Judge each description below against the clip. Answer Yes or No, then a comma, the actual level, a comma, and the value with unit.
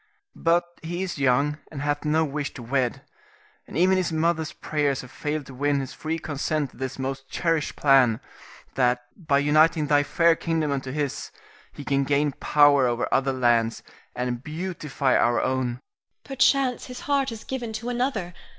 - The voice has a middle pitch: Yes, medium, 145 Hz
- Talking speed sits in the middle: Yes, average, 175 wpm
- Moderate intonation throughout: Yes, average, 3.8 semitones